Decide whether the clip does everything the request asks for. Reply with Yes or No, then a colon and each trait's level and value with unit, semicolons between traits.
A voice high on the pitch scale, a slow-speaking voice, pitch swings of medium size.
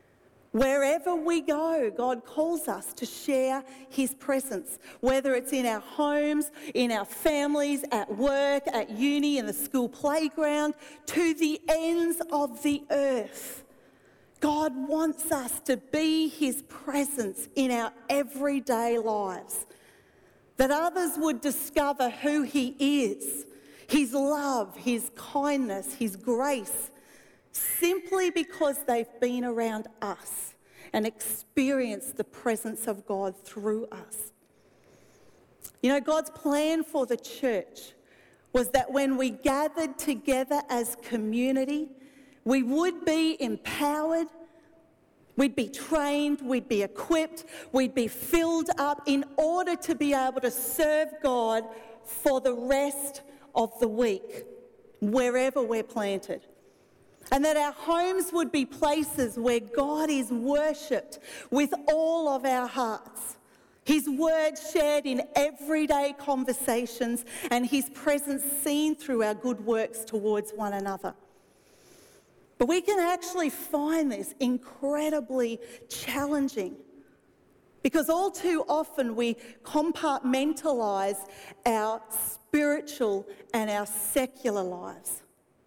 Yes: very high, 275 Hz; slow, 120 wpm; average, 3.9 semitones